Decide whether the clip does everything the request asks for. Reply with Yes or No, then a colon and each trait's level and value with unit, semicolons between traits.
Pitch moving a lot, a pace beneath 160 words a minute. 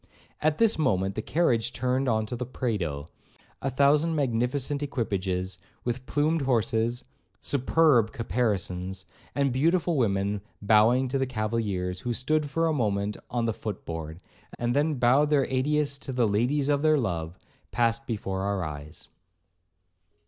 Yes: wide, 5.7 semitones; average, 145 wpm